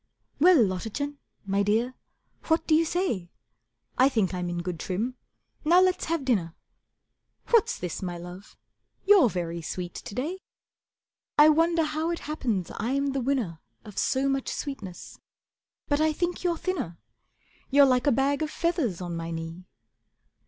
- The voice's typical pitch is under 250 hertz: No, very high, 260 Hz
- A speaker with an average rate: Yes, average, 155 wpm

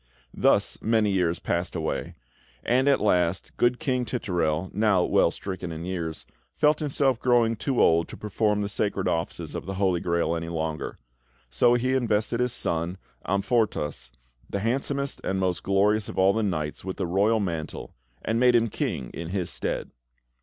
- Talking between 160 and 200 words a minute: Yes, average, 170 wpm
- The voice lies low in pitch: Yes, low, 100 Hz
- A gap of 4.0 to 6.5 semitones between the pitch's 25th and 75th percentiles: Yes, average, 5.2 semitones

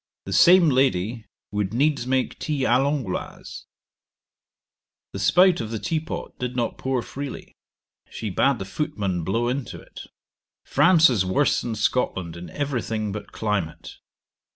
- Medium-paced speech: Yes, average, 150 wpm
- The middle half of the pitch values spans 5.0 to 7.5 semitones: Yes, wide, 5.5 semitones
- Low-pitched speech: Yes, low, 120 Hz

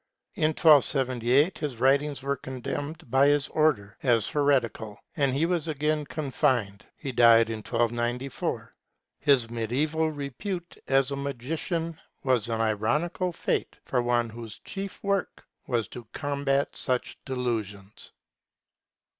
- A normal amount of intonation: Yes, average, 4.2 semitones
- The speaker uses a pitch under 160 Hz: Yes, low, 135 Hz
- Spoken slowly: Yes, slow, 125 wpm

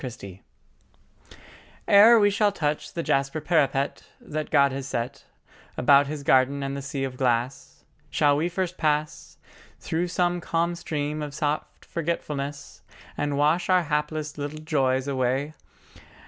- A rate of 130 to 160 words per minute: Yes, average, 145 wpm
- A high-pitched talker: No, medium, 145 Hz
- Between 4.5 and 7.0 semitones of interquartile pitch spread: No, average, 3.0 semitones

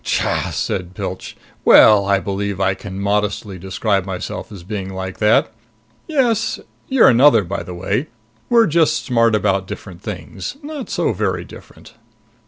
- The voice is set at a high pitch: No, low, 100 Hz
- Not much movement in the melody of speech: No, average, 3.8 semitones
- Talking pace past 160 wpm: No, average, 150 wpm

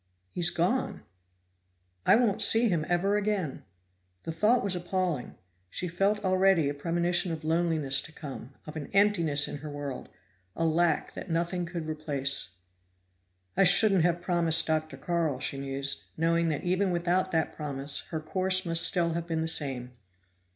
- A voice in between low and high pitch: Yes, medium, 170 Hz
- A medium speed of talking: Yes, average, 160 wpm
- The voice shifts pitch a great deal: No, average, 3.1 semitones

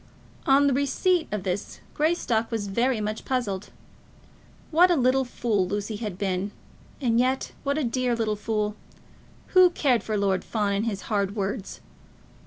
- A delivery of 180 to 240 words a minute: No, average, 155 wpm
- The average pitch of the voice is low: No, high, 225 Hz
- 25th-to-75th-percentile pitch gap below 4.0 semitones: No, average, 4.5 semitones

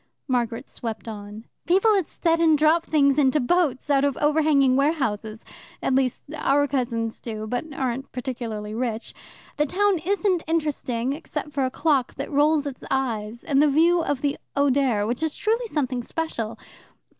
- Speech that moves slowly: No, average, 160 wpm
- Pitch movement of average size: Yes, average, 4.4 semitones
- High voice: Yes, very high, 275 Hz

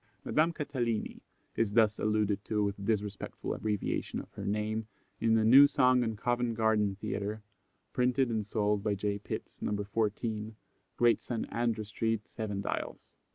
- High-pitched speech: No, low, 110 Hz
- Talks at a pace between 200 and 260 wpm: No, average, 155 wpm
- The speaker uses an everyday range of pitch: No, narrow, 2.0 semitones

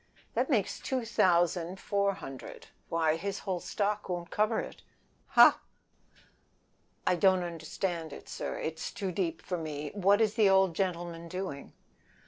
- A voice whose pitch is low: No, medium, 180 Hz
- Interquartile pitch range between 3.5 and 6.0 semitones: No, average, 3.1 semitones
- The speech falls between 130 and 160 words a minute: Yes, average, 140 wpm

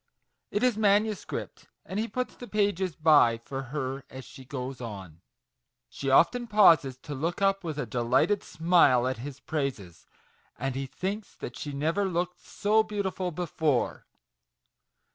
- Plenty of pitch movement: Yes, wide, 7.1 semitones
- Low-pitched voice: No, medium, 155 Hz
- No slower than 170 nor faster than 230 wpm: No, average, 150 wpm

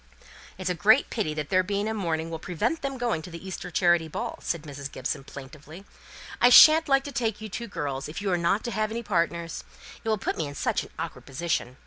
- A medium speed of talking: No, fast, 240 wpm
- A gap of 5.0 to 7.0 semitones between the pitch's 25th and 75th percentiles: Yes, wide, 5.6 semitones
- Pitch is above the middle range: No, medium, 180 Hz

